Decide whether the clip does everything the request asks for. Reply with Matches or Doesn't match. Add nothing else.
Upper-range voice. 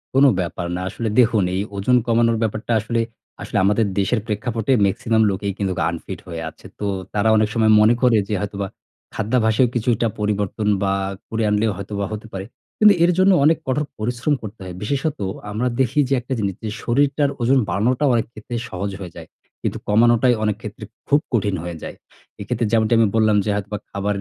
Doesn't match